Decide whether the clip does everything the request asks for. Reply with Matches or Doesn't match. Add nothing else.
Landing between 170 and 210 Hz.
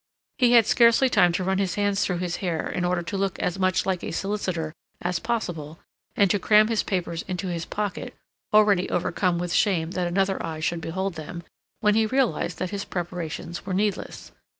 Matches